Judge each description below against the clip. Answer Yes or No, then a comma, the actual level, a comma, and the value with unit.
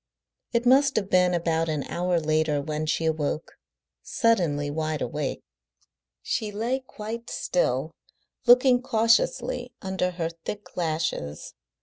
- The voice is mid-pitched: Yes, medium, 180 Hz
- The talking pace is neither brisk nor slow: No, slow, 120 wpm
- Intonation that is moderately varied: No, wide, 6.7 semitones